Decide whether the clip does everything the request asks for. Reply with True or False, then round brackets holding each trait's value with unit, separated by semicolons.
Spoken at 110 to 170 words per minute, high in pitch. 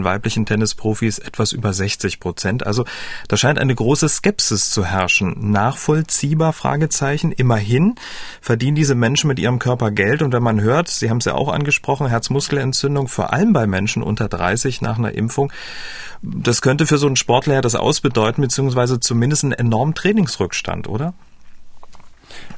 False (155 wpm; 125 Hz)